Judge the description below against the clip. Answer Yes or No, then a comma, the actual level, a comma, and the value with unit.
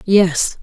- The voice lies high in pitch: No, medium, 180 Hz